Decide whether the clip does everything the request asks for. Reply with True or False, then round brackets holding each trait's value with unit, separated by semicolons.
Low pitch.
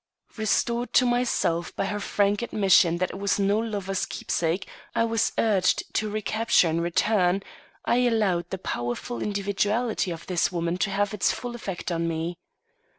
False (195 Hz)